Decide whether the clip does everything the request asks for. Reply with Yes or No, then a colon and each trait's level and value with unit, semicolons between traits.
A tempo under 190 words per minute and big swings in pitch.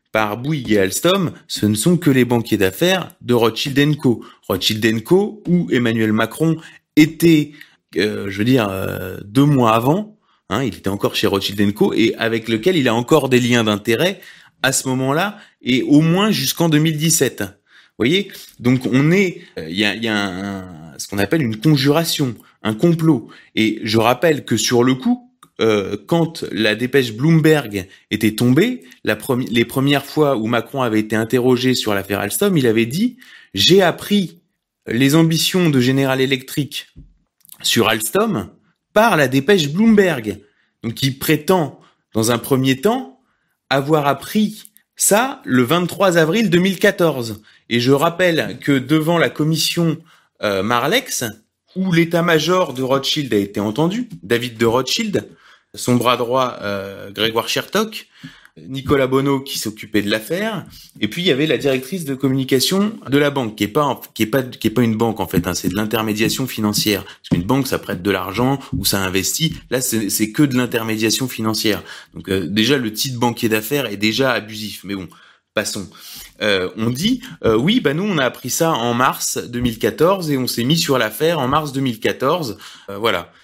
Yes: average, 175 wpm; wide, 6.4 semitones